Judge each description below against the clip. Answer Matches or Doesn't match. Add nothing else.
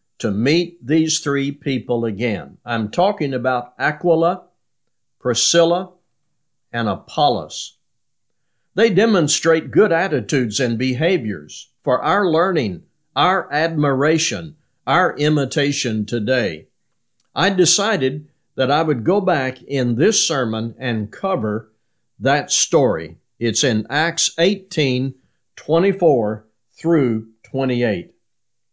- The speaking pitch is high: Doesn't match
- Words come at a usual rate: Doesn't match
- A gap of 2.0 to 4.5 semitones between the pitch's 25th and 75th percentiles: Doesn't match